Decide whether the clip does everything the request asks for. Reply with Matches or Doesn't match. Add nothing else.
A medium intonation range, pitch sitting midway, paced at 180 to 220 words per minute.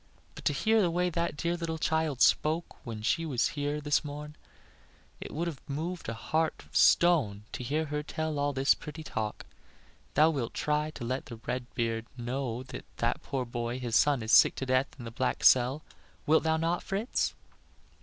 Matches